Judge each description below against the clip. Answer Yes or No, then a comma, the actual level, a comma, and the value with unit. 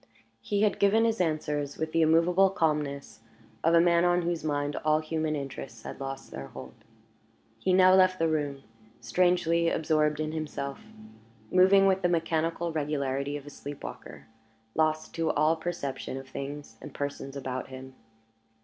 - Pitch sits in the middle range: Yes, medium, 155 Hz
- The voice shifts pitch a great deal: No, average, 3.4 semitones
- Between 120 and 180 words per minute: Yes, average, 160 wpm